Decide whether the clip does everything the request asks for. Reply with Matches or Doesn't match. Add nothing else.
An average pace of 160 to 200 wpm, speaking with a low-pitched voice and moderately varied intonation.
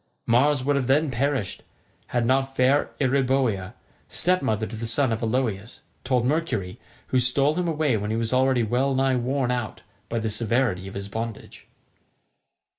Matches